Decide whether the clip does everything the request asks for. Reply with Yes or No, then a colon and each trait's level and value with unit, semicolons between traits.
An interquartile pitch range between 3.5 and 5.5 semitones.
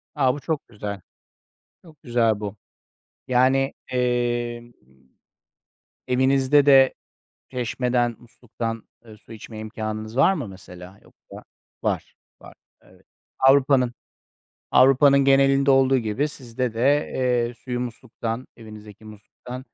No: average, 3.0 semitones